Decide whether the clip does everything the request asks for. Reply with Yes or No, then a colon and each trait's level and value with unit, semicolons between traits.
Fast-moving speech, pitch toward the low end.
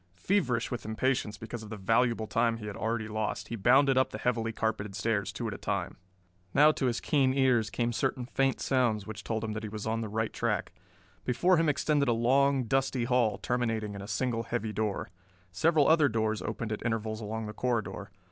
Yes: fast, 210 wpm; low, 115 Hz